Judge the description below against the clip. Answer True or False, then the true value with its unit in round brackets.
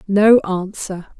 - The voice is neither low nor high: False (195 Hz)